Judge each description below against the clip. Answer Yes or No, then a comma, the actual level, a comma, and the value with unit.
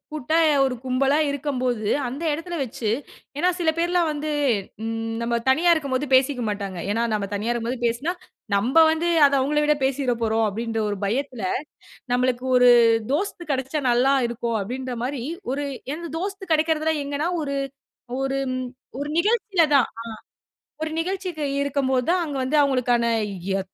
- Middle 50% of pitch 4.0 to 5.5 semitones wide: Yes, average, 4.4 semitones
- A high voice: Yes, very high, 270 Hz